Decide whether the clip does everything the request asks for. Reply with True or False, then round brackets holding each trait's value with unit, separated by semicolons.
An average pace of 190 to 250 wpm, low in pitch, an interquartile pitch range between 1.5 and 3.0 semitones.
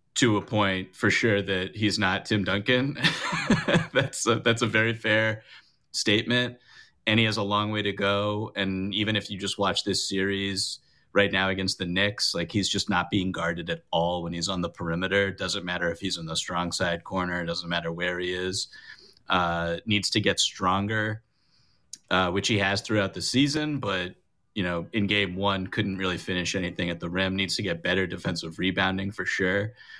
True (200 wpm; 100 Hz; 2.4 semitones)